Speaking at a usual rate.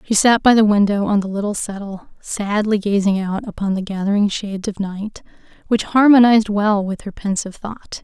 Yes: average, 185 wpm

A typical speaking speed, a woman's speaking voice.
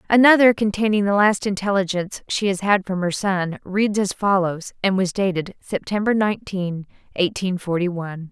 Yes: average, 160 wpm; female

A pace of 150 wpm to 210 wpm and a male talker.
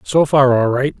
No: fast, 240 wpm; male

